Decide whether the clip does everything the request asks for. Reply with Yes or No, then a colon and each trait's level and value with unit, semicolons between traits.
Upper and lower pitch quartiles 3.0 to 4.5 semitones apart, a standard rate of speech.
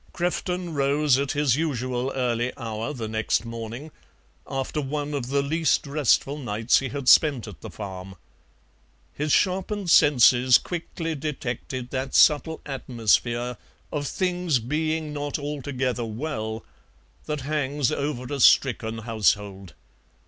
No: average, 4.0 semitones; slow, 125 wpm